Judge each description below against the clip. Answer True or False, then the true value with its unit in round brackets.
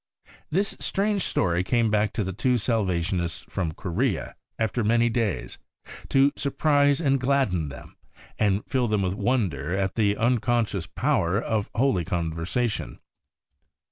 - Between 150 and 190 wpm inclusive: False (135 wpm)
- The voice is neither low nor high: False (110 Hz)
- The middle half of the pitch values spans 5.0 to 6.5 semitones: True (5.5 semitones)